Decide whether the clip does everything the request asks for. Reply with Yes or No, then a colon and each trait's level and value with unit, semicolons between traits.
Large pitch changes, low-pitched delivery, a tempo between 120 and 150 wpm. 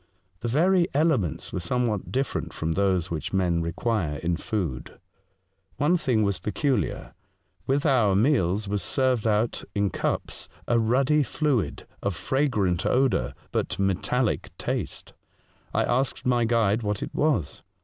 Yes: wide, 5.7 semitones; low, 110 Hz; average, 140 wpm